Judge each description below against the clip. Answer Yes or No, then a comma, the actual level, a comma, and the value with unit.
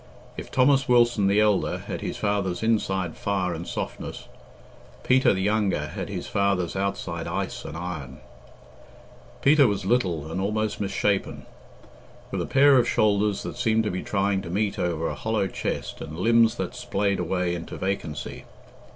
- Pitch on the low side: Yes, low, 100 Hz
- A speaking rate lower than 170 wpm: Yes, average, 160 wpm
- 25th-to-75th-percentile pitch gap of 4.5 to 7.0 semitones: No, average, 3.4 semitones